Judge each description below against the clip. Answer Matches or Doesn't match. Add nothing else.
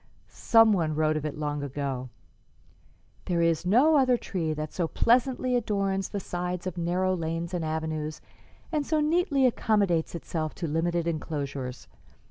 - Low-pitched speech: Doesn't match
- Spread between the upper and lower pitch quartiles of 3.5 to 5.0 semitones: Doesn't match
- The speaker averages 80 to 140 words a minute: Doesn't match